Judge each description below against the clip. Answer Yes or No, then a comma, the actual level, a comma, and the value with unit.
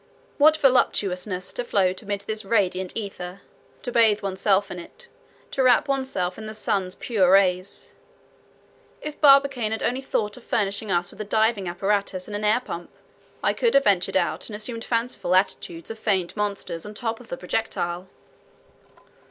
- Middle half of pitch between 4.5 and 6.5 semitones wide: No, average, 3.7 semitones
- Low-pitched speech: No, high, 205 Hz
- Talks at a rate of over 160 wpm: Yes, average, 170 wpm